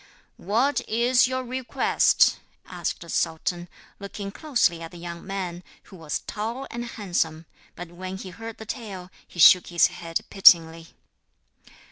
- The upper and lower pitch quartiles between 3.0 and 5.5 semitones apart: Yes, average, 5.0 semitones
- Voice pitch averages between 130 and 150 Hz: No, high, 190 Hz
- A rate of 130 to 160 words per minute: Yes, average, 145 wpm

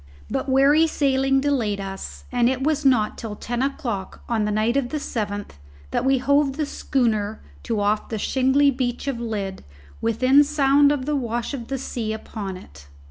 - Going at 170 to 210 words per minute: Yes, average, 185 wpm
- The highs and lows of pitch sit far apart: No, average, 4.3 semitones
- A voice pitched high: Yes, very high, 250 Hz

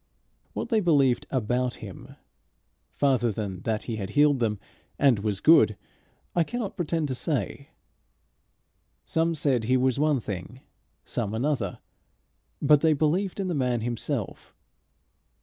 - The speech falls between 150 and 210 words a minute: No, slow, 135 wpm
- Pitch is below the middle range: Yes, low, 130 Hz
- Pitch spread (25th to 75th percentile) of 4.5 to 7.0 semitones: Yes, wide, 5.5 semitones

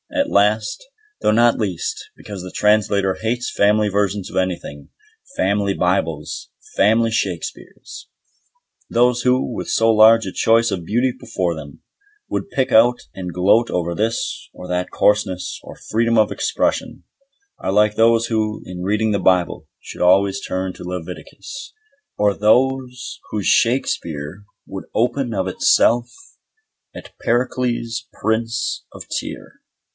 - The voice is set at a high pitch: No, low, 105 Hz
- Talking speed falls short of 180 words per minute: Yes, slow, 135 wpm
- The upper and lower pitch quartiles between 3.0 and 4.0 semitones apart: Yes, average, 3.7 semitones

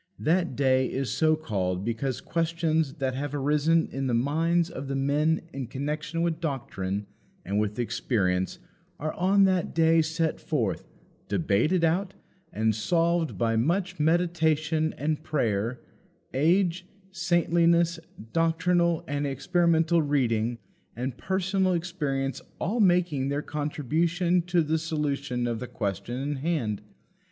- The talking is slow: Yes, slow, 130 wpm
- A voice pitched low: No, medium, 155 Hz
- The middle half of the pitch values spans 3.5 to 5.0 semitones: Yes, average, 4.5 semitones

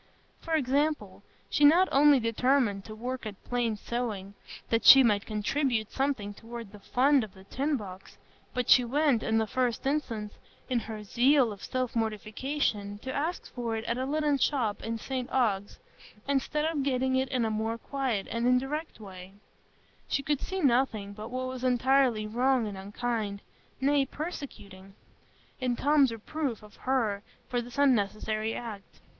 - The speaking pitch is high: Yes, high, 245 Hz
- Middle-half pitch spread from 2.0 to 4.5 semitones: Yes, average, 4.0 semitones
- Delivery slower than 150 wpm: No, average, 165 wpm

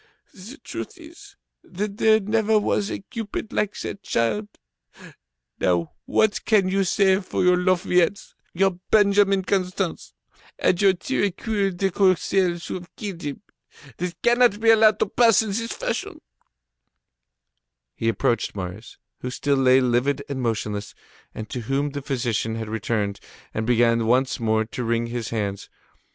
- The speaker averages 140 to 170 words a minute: Yes, average, 150 wpm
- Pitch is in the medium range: Yes, medium, 180 Hz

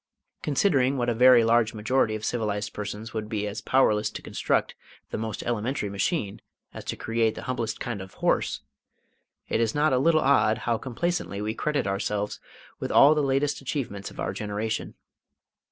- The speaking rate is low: No, average, 175 wpm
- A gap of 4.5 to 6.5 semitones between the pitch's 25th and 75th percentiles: No, average, 4.0 semitones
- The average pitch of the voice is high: No, low, 115 Hz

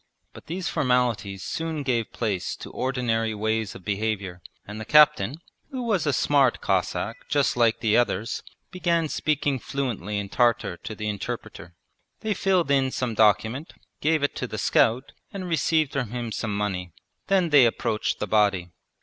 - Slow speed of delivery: No, average, 165 wpm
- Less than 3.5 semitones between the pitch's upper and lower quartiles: No, wide, 5.6 semitones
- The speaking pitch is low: Yes, low, 120 Hz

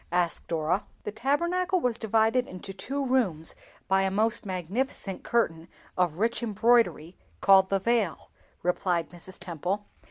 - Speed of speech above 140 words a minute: No, slow, 135 wpm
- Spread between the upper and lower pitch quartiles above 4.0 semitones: Yes, average, 4.8 semitones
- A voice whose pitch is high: Yes, high, 195 Hz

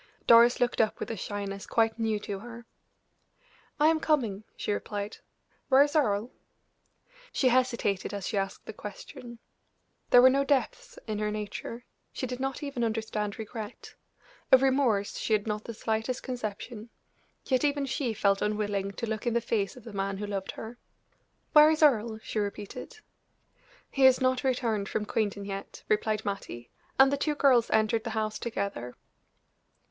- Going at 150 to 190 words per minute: Yes, average, 170 wpm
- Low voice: No, high, 225 Hz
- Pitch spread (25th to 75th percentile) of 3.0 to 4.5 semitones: Yes, average, 3.8 semitones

